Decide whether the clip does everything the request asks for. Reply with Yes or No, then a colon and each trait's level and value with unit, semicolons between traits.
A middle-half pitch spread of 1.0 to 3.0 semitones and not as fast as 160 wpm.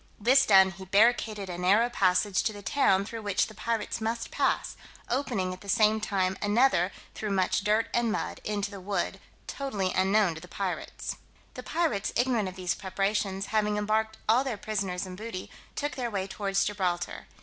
No: average, 2.7 semitones; average, 185 wpm